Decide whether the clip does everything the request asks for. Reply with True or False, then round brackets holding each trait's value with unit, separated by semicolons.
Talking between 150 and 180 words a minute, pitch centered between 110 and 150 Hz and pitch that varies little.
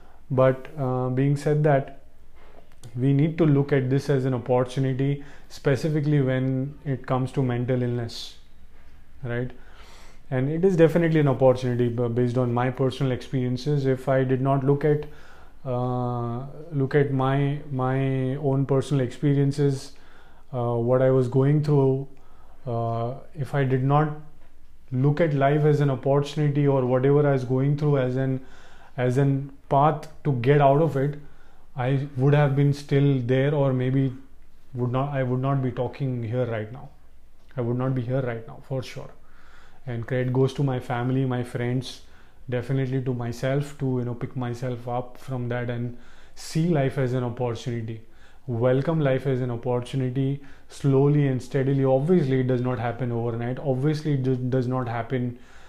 True (165 wpm; 130 Hz; 2.1 semitones)